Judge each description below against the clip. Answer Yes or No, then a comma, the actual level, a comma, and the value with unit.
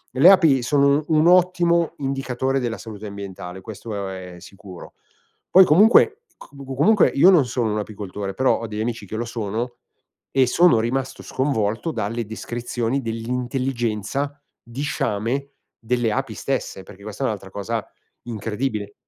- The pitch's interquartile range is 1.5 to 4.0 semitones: No, average, 4.5 semitones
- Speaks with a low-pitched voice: Yes, low, 120 Hz